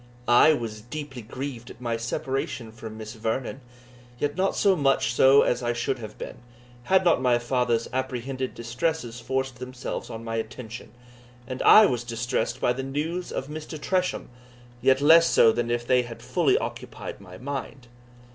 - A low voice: Yes, low, 125 Hz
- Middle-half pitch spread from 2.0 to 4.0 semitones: Yes, average, 2.8 semitones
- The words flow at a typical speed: Yes, average, 170 wpm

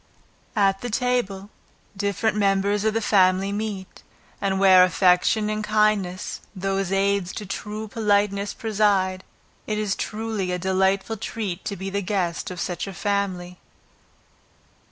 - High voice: Yes, high, 200 Hz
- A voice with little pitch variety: Yes, narrow, 2.0 semitones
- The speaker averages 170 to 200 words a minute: No, slow, 135 wpm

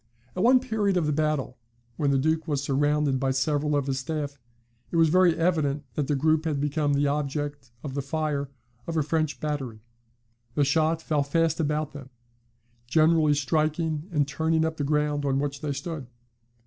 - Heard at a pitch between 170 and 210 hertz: No, medium, 150 Hz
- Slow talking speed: No, average, 185 wpm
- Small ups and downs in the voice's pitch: Yes, narrow, 2.1 semitones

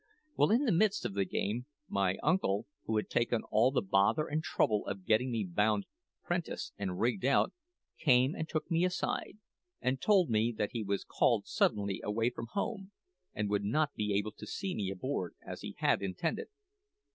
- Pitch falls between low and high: No, low, 115 Hz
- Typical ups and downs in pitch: No, wide, 7.4 semitones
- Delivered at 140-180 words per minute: No, average, 190 wpm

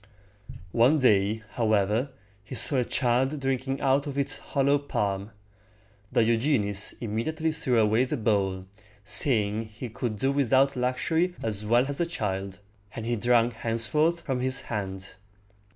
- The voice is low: Yes, low, 120 Hz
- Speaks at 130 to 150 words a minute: Yes, average, 140 wpm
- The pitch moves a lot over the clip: No, average, 4.4 semitones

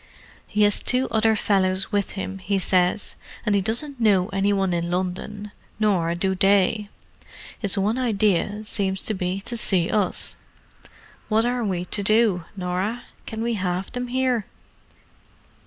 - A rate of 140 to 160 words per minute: Yes, average, 155 wpm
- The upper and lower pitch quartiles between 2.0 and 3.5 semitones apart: Yes, average, 2.8 semitones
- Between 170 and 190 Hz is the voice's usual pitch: No, high, 200 Hz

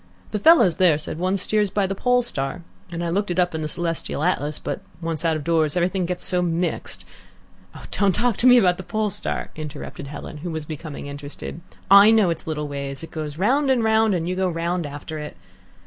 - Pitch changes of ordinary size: Yes, average, 4.1 semitones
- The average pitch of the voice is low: No, medium, 175 Hz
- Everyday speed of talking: No, fast, 225 wpm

